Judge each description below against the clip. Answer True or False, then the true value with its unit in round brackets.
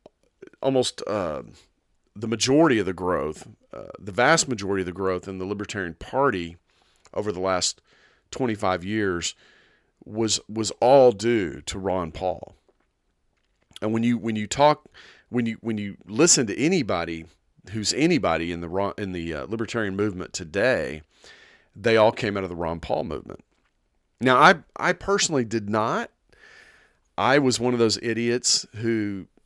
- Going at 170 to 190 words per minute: False (155 wpm)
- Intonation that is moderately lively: True (4.0 semitones)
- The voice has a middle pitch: False (105 Hz)